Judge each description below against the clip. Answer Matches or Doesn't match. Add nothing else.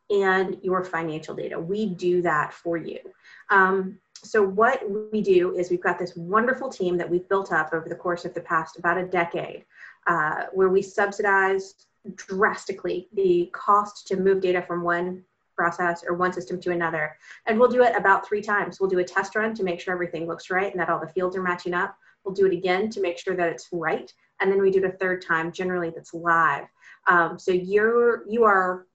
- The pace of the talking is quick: Matches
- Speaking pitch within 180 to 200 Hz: Matches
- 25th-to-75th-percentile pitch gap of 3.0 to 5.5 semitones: Doesn't match